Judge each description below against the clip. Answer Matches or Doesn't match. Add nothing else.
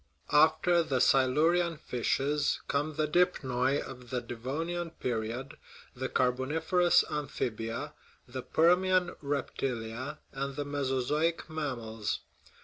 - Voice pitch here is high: Doesn't match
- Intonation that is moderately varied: Matches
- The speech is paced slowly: Matches